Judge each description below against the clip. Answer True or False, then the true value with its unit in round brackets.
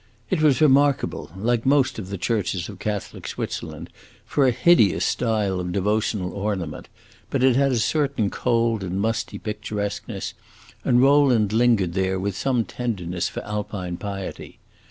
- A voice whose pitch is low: True (110 Hz)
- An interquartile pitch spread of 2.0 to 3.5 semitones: False (4.3 semitones)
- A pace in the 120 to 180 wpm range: True (150 wpm)